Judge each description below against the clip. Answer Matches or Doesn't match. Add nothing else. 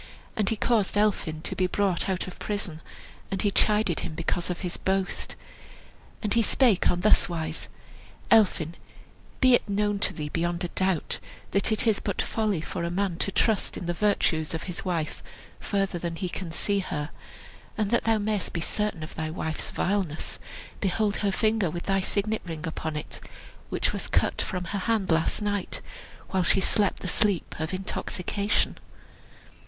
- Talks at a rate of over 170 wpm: Matches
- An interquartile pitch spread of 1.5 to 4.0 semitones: Matches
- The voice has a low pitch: Doesn't match